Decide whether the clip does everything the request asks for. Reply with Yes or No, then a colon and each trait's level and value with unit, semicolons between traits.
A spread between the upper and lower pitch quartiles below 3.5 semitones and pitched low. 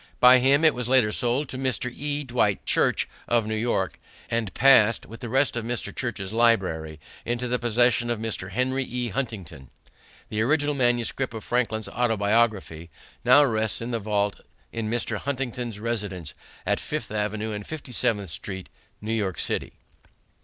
Yes: average, 3.0 semitones; low, 115 Hz